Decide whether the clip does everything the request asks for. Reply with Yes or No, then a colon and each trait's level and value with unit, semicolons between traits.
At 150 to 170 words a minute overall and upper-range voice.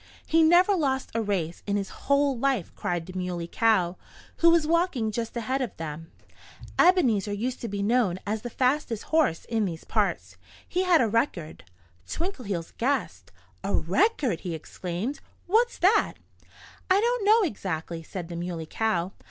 Yes: average, 160 wpm; high, 225 Hz